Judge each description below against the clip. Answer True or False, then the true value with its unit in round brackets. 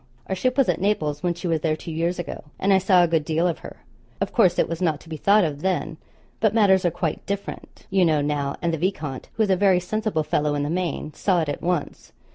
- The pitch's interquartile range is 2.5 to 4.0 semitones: True (3.5 semitones)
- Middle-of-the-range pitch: True (175 Hz)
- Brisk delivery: True (260 wpm)